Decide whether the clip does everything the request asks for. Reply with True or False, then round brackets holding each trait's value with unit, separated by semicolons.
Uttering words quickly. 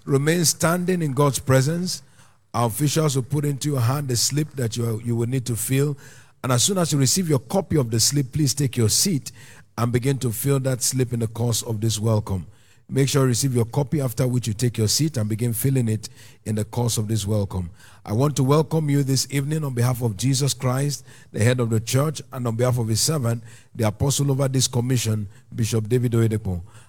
True (225 wpm)